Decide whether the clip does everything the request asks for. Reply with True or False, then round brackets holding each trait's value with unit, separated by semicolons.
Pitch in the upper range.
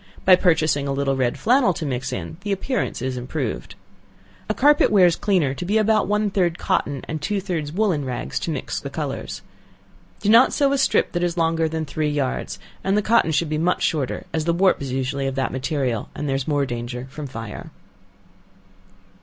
False (155 Hz)